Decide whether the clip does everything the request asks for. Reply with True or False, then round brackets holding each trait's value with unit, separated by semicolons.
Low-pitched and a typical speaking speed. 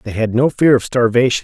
False (120 Hz; 250 wpm)